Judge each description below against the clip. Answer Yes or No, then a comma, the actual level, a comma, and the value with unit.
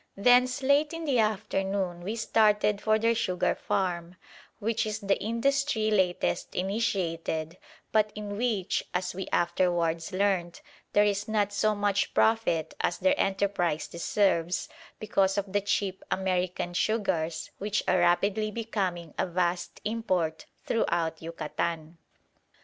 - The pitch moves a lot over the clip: No, average, 3.7 semitones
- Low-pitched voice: No, high, 195 Hz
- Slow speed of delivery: Yes, slow, 130 wpm